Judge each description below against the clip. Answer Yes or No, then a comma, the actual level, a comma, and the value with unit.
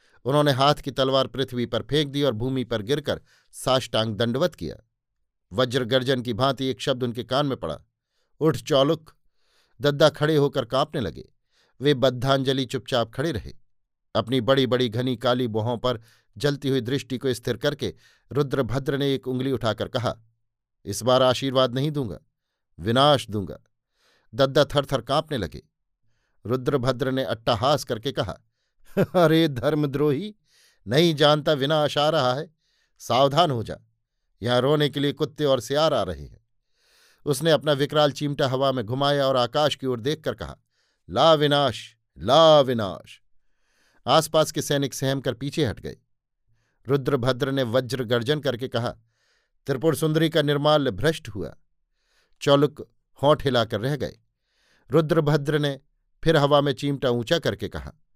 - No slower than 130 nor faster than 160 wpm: Yes, average, 150 wpm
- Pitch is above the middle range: No, low, 135 Hz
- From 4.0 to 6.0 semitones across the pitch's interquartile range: No, average, 3.3 semitones